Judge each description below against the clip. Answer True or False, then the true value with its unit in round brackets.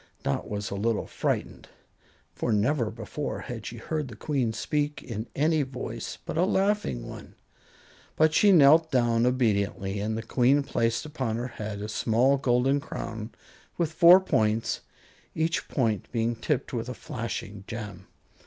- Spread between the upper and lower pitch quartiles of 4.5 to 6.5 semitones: True (4.8 semitones)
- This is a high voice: False (120 Hz)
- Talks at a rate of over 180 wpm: False (155 wpm)